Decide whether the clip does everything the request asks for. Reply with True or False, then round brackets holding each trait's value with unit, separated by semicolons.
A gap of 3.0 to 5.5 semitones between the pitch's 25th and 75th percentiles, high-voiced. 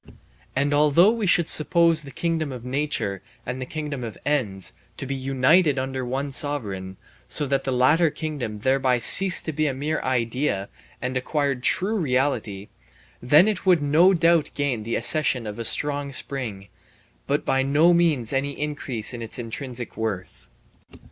False (3.8 semitones; 135 Hz)